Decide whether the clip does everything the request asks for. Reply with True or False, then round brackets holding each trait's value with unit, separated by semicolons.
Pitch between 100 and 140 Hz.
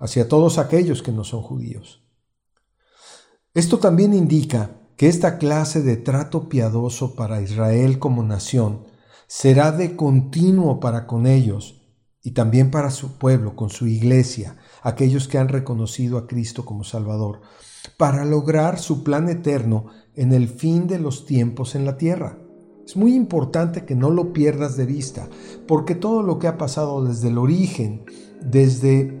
True (135 Hz)